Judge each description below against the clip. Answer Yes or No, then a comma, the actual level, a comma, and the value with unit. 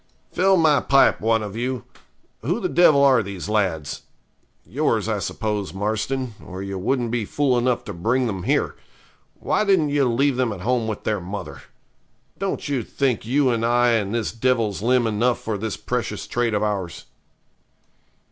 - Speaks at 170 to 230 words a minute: Yes, average, 175 wpm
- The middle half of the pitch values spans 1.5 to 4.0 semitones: Yes, average, 3.7 semitones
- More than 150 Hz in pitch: No, low, 115 Hz